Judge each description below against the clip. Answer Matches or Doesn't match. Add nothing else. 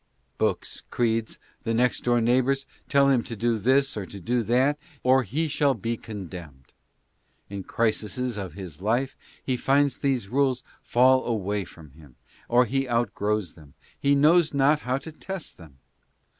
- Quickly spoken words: Doesn't match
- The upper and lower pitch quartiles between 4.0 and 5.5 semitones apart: Matches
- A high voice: Doesn't match